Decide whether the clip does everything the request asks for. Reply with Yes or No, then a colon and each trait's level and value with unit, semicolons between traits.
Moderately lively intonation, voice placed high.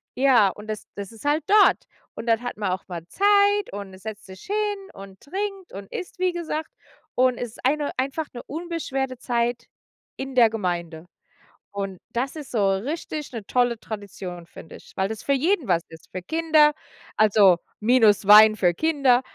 No: wide, 7.2 semitones; high, 240 Hz